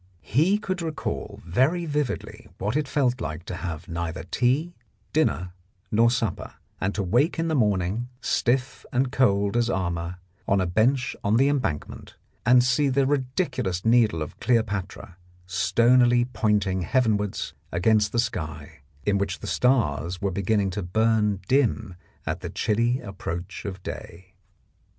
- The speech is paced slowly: No, average, 145 wpm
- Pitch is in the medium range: No, low, 110 Hz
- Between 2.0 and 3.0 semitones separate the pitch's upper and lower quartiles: No, wide, 5.4 semitones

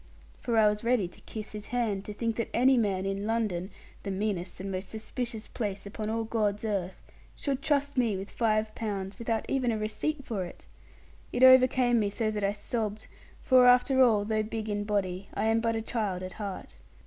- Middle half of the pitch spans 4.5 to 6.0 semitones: No, average, 2.7 semitones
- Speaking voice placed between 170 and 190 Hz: No, high, 215 Hz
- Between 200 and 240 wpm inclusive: Yes, fast, 205 wpm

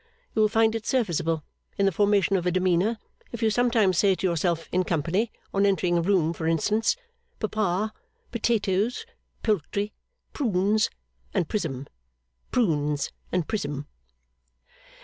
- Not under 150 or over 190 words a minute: No, slow, 135 wpm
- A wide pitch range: No, average, 4.2 semitones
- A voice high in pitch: Yes, high, 195 Hz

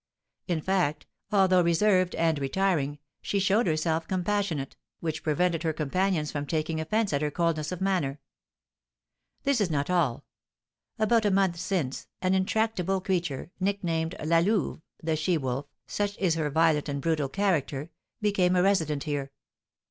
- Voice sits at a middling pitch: Yes, medium, 170 Hz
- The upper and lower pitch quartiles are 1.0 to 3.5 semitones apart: No, average, 3.9 semitones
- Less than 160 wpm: Yes, average, 150 wpm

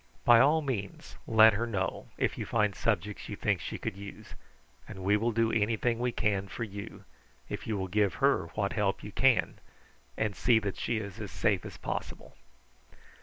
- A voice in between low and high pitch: No, low, 105 Hz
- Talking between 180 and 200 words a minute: Yes, average, 190 wpm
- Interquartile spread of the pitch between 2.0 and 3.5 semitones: Yes, narrow, 2.5 semitones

